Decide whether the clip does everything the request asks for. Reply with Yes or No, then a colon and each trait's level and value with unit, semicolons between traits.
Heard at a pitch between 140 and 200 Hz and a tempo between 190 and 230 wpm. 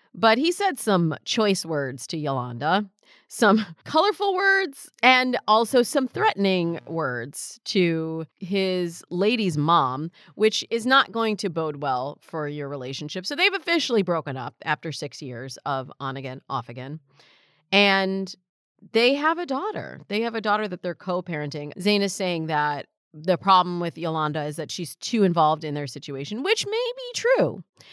No: medium, 185 Hz; average, 165 wpm